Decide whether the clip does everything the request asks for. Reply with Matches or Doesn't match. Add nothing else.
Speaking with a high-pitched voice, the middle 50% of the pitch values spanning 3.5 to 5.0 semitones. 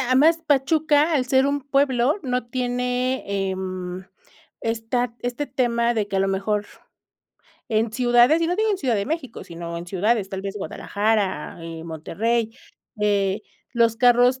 Matches